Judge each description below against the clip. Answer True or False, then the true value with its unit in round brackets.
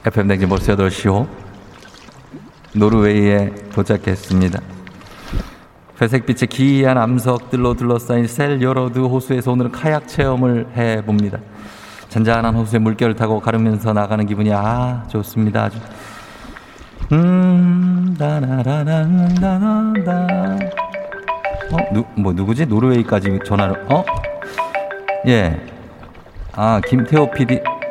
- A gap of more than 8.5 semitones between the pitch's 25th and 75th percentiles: False (5.6 semitones)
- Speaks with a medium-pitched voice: False (115 Hz)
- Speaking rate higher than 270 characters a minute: False (245 characters per minute)